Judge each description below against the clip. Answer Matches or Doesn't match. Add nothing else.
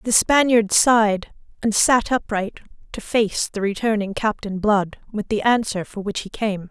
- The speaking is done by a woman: Matches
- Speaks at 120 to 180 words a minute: Matches